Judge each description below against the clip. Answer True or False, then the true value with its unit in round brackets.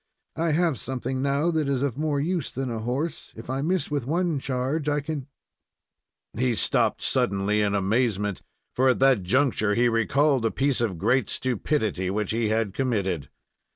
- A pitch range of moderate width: True (4.7 semitones)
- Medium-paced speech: True (180 wpm)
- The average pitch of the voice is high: False (130 Hz)